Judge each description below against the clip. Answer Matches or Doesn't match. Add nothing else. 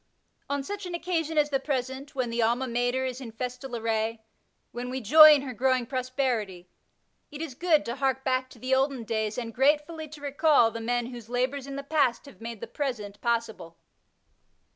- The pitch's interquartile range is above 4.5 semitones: Doesn't match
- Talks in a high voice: Matches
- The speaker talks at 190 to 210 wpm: Matches